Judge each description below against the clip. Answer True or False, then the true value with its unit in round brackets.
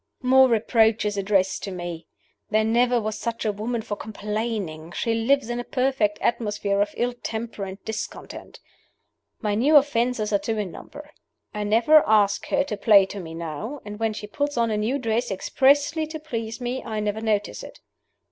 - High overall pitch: True (220 Hz)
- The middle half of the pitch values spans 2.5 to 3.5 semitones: True (2.9 semitones)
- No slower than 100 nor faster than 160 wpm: False (185 wpm)